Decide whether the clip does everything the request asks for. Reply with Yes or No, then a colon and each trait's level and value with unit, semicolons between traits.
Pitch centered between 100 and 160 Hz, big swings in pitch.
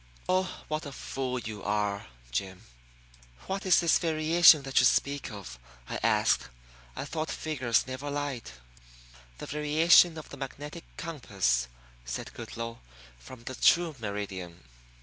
Yes: low, 135 Hz; wide, 7.2 semitones